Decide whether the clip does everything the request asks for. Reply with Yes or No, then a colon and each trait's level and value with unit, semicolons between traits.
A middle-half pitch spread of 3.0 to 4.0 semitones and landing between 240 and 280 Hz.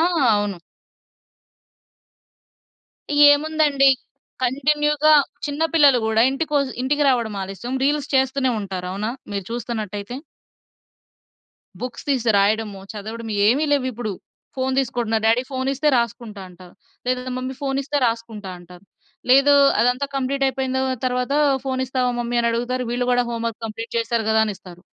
Yes: average, 3.5 semitones; high, 245 Hz